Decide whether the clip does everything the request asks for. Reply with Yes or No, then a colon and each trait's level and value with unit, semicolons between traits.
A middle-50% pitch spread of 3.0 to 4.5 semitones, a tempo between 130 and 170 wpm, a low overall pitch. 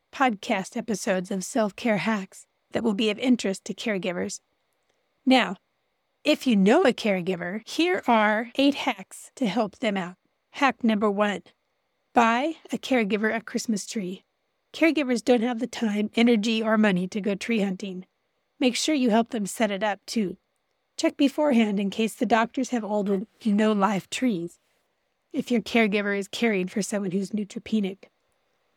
No: average, 3.3 semitones; average, 165 wpm; high, 220 Hz